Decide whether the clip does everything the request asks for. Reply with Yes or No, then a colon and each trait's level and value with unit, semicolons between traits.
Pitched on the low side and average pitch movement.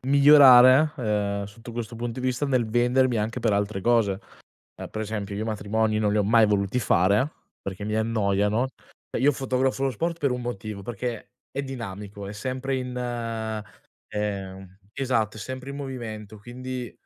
Yes: low, 115 Hz; average, 3.6 semitones